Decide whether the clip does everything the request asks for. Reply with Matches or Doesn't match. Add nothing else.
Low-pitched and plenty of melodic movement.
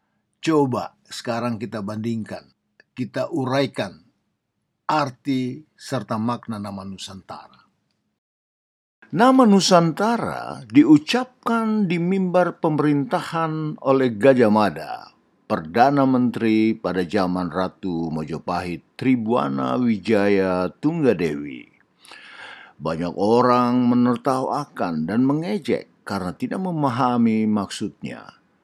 Matches